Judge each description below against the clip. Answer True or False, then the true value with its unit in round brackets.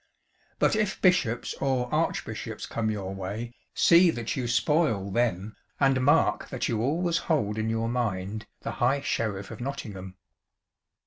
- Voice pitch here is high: False (120 Hz)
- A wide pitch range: False (4.8 semitones)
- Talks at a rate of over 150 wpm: False (145 wpm)